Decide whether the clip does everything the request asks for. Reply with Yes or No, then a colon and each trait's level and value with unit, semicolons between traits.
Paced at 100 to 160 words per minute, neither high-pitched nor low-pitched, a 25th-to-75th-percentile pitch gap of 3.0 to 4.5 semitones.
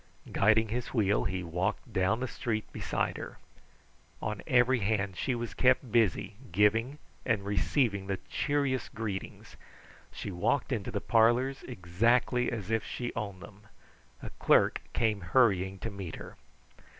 No: average, 145 wpm; low, 110 Hz; average, 3.7 semitones